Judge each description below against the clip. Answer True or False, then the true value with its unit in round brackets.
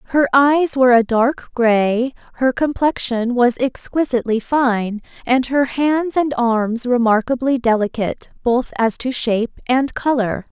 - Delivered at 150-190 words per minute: False (135 wpm)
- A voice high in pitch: True (250 Hz)